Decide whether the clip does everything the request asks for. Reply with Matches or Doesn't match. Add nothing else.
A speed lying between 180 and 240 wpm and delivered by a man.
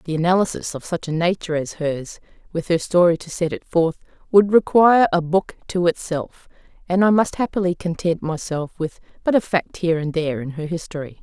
Doesn't match